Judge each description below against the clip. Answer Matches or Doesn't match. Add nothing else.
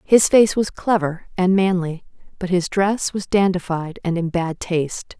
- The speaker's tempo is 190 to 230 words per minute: Doesn't match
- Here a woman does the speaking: Matches